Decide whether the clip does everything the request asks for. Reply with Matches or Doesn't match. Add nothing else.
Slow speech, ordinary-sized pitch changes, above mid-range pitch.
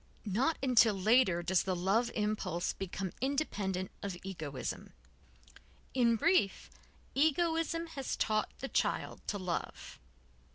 Doesn't match